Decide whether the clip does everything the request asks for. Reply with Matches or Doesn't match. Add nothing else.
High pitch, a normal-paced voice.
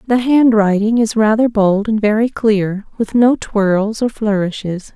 Matches